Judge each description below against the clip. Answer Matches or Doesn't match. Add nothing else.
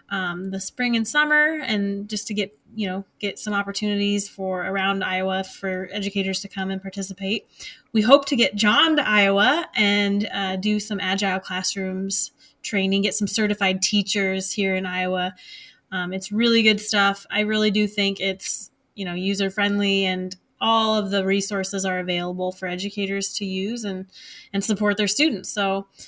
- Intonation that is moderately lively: Doesn't match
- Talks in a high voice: Matches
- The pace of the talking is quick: Doesn't match